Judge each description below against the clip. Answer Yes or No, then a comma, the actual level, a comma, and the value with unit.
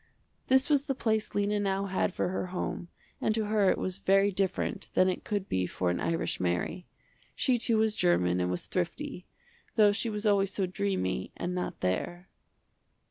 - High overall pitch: Yes, high, 195 Hz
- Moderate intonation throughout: Yes, average, 3.3 semitones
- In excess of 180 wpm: Yes, average, 190 wpm